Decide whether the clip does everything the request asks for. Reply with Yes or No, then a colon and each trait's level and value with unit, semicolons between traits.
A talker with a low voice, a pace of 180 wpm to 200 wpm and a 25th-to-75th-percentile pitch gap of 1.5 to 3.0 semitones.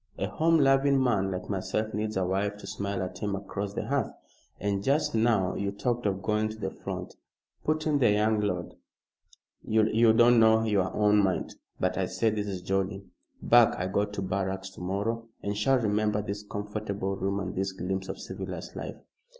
Yes: low, 105 Hz; average, 190 wpm; narrow, 2.4 semitones